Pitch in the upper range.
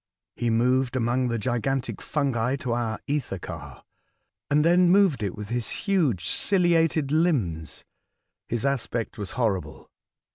No: low, 125 Hz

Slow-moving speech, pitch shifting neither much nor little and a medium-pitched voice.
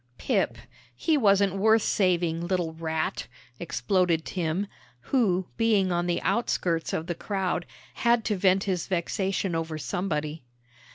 Yes: slow, 130 wpm; average, 3.1 semitones; medium, 180 Hz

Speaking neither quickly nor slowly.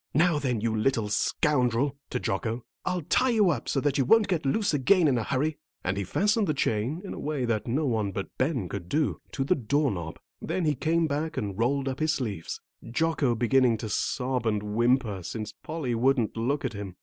No: fast, 215 wpm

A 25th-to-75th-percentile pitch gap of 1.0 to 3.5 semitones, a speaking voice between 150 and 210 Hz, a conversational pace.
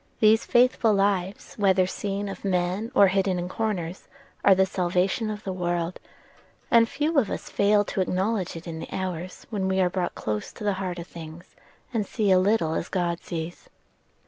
Yes: narrow, 2.6 semitones; high, 190 Hz; average, 190 wpm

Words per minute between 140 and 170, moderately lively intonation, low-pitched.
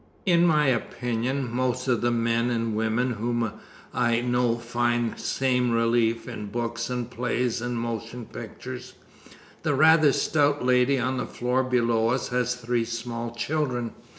No: average, 150 wpm; narrow, 1.4 semitones; low, 120 Hz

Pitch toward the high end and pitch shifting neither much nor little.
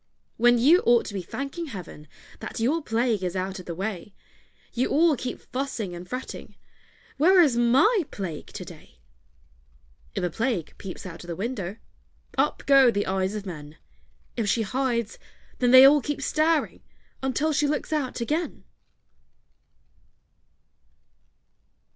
No: high, 235 Hz; wide, 6.5 semitones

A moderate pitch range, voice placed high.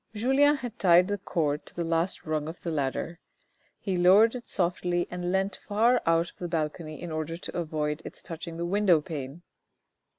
No: average, 3.3 semitones; medium, 175 Hz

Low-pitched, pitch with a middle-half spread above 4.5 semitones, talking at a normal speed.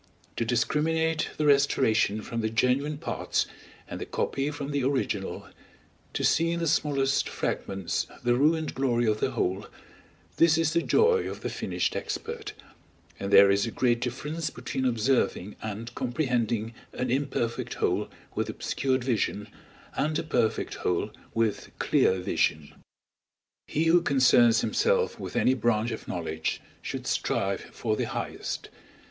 Yes: low, 125 Hz; wide, 5.5 semitones; average, 145 wpm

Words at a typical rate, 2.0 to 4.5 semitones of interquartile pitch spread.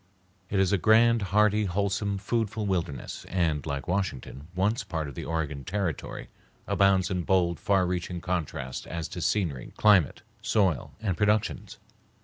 Yes: average, 150 wpm; average, 3.7 semitones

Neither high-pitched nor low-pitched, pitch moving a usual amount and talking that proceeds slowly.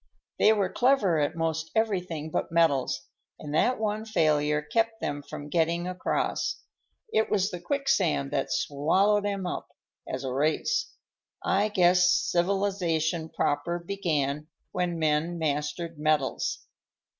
Yes: medium, 170 Hz; average, 4.7 semitones; slow, 130 wpm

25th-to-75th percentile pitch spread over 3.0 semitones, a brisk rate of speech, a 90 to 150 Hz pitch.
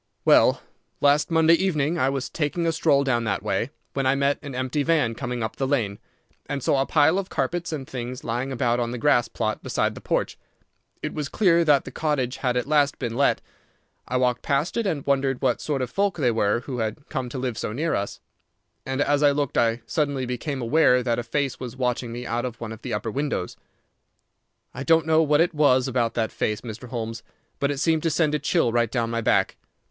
Yes: average, 3.8 semitones; fast, 225 wpm; low, 135 Hz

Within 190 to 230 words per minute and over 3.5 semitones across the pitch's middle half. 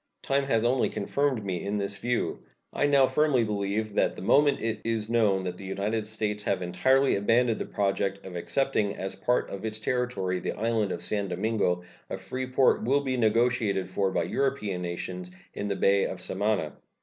Yes: average, 195 wpm; average, 4.0 semitones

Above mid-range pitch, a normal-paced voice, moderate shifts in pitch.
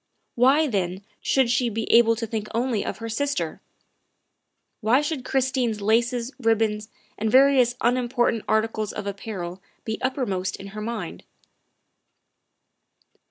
No: high, 230 Hz; slow, 130 wpm; average, 3.0 semitones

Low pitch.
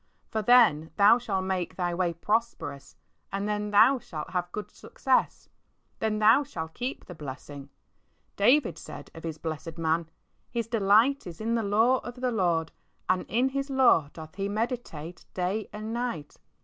No: high, 205 Hz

